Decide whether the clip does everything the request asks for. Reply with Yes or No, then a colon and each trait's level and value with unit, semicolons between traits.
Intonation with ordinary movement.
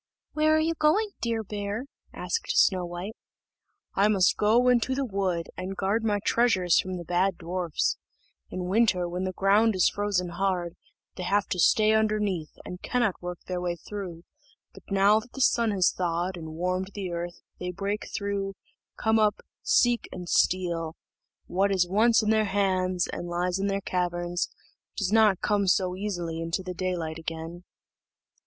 Yes: average, 3.1 semitones